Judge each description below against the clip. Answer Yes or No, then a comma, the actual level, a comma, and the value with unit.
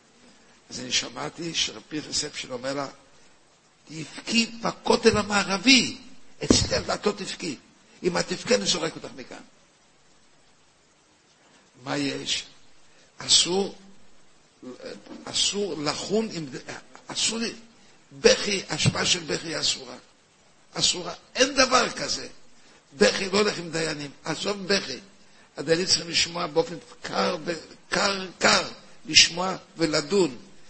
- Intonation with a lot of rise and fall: Yes, wide, 5.9 semitones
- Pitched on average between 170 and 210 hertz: Yes, medium, 185 Hz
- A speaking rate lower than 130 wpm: Yes, average, 105 wpm